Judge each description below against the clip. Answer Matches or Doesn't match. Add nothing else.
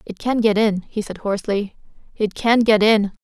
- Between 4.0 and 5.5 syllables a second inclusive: Matches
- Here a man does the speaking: Doesn't match